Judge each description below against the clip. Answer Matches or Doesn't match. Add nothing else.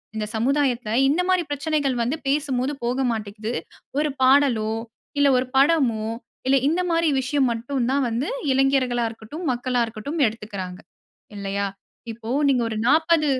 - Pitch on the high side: Matches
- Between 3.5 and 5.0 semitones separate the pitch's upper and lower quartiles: Matches